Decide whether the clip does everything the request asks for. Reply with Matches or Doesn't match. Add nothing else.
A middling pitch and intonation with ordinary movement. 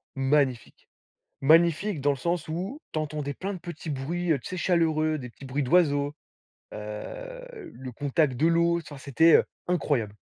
Matches